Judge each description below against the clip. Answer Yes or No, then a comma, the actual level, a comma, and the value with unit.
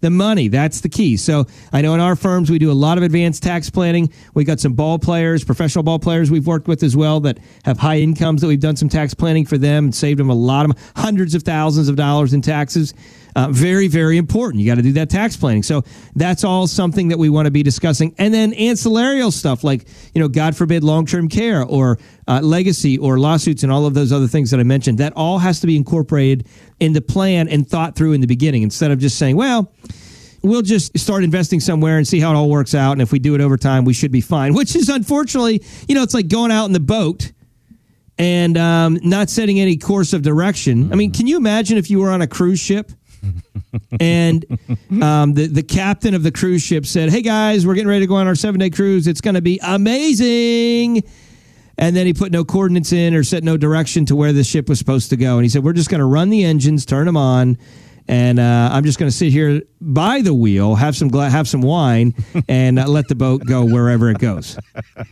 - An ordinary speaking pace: No, fast, 245 wpm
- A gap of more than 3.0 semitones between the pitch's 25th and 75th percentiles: Yes, average, 4.7 semitones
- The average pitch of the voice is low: No, medium, 155 Hz